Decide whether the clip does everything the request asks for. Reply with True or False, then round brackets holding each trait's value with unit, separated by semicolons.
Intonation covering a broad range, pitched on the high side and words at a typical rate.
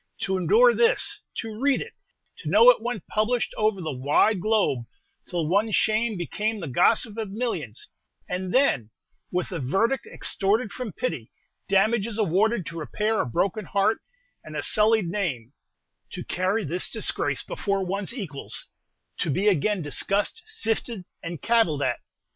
False (4.5 semitones; 205 Hz; 155 wpm)